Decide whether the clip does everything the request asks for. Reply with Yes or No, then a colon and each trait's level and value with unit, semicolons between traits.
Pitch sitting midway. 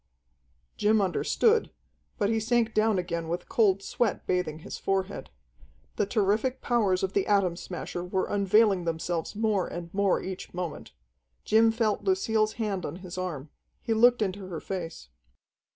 No: high, 195 Hz